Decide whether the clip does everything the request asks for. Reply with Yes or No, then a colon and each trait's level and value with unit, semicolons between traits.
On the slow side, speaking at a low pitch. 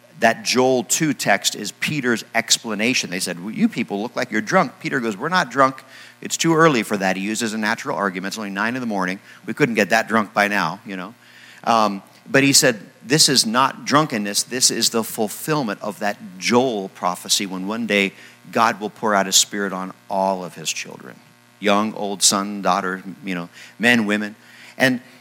No: average, 200 wpm; low, 105 Hz